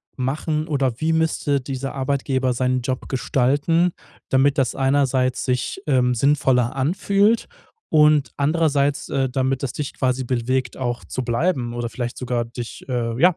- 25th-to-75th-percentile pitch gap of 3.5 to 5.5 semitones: No, narrow, 2.4 semitones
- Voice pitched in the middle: No, low, 130 Hz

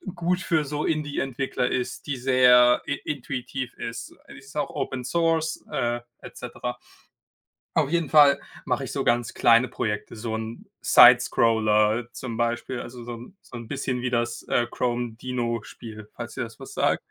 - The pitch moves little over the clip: No, average, 3.1 semitones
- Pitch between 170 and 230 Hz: No, low, 125 Hz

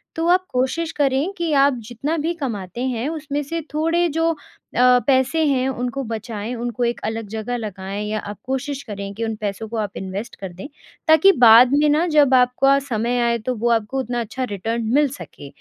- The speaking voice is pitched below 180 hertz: No, very high, 250 Hz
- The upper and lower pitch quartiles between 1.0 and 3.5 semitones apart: No, average, 4.4 semitones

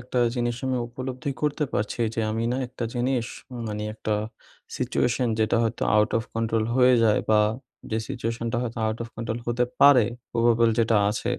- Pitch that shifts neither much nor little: No, narrow, 1.8 semitones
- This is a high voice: No, low, 115 Hz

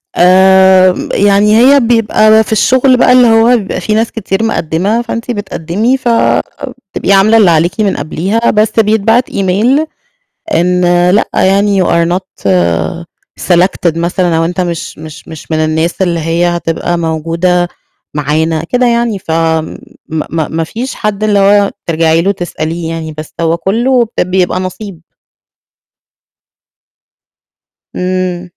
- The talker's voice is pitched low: No, medium, 185 Hz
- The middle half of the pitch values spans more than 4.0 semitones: Yes, average, 4.5 semitones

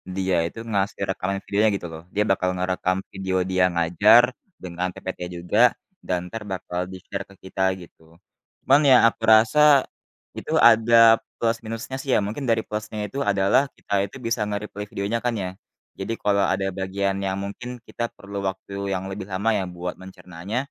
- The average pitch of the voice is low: Yes, low, 100 Hz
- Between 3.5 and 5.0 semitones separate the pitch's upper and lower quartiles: No, average, 2.7 semitones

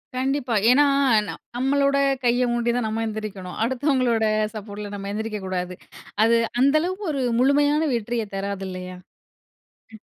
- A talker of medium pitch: No, high, 235 Hz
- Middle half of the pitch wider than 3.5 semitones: Yes, average, 4.6 semitones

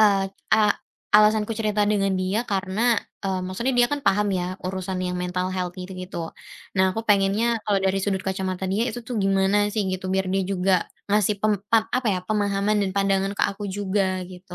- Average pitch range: No, narrow, 1.8 semitones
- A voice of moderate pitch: No, high, 195 Hz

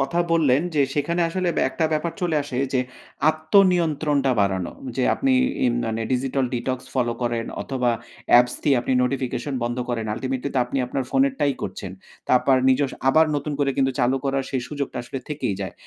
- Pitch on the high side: No, low, 135 Hz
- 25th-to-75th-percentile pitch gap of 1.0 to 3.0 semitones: No, average, 3.5 semitones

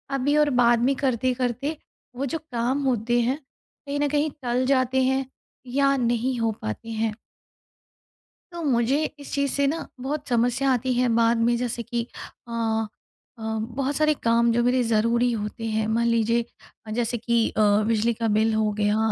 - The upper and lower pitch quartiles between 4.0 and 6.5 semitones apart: No, average, 2.7 semitones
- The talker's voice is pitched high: Yes, high, 240 Hz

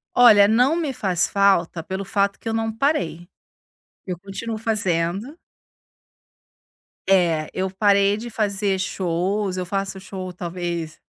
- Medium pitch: No, high, 195 Hz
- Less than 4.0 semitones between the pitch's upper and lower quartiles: Yes, average, 3.2 semitones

